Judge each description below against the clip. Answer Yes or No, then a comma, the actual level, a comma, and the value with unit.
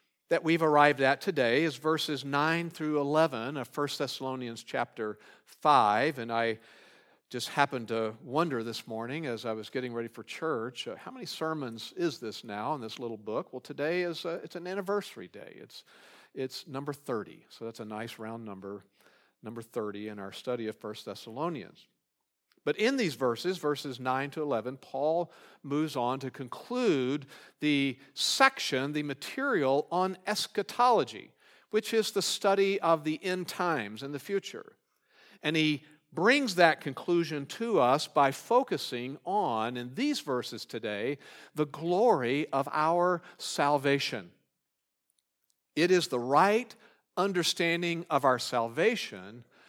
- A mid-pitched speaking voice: Yes, medium, 145 Hz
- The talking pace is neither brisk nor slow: Yes, average, 150 wpm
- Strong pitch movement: Yes, wide, 5.7 semitones